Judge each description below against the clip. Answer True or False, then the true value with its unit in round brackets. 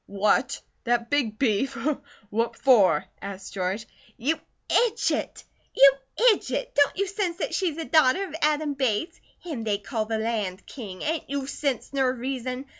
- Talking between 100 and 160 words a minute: True (155 wpm)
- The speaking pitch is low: False (260 Hz)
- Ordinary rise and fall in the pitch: False (5.8 semitones)